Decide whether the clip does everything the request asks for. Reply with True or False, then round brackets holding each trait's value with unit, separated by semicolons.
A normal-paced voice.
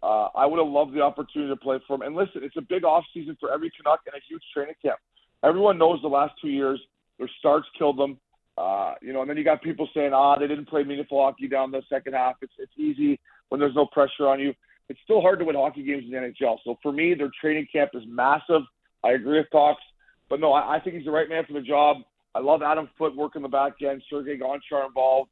False (260 wpm)